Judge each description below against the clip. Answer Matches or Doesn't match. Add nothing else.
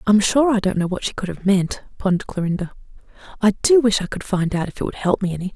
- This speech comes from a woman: Matches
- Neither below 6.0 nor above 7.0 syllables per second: Matches